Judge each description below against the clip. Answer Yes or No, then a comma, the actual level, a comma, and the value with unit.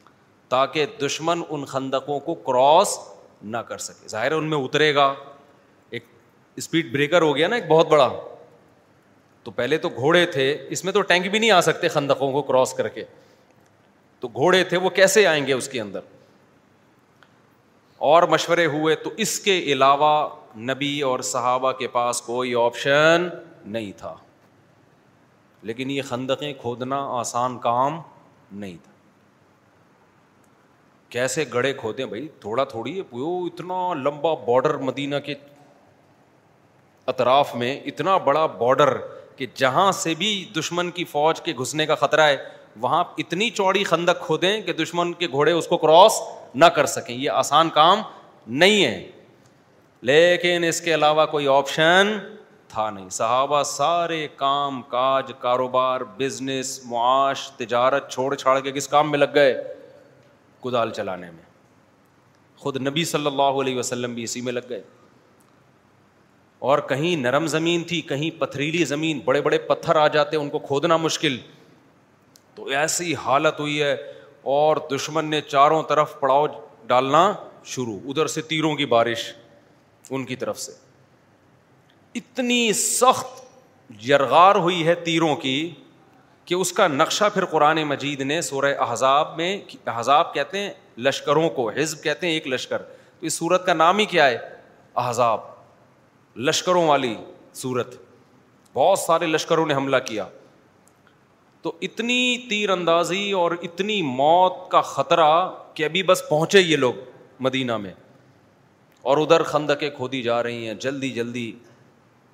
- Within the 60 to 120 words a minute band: No, average, 145 wpm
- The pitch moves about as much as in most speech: Yes, average, 4.2 semitones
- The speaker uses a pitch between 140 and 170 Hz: Yes, medium, 150 Hz